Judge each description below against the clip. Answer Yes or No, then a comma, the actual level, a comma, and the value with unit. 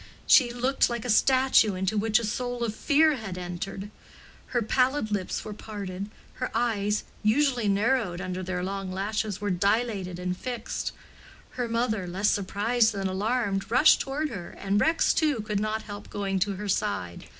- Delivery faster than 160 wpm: Yes, average, 170 wpm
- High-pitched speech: Yes, high, 210 Hz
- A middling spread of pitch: Yes, average, 3.8 semitones